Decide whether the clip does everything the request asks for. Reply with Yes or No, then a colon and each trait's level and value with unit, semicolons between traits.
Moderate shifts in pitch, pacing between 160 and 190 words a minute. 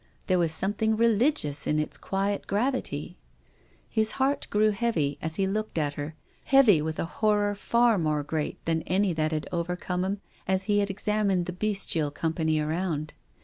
Yes: average, 4.9 semitones; average, 170 wpm